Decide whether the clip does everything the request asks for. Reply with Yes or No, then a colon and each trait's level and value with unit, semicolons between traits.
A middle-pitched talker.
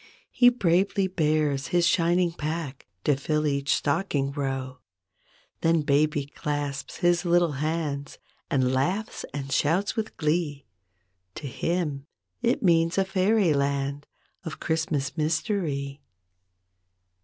Yes: medium, 155 Hz